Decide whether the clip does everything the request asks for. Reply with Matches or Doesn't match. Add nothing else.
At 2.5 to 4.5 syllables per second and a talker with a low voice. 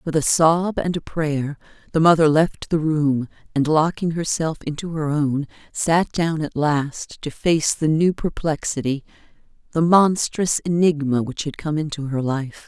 Doesn't match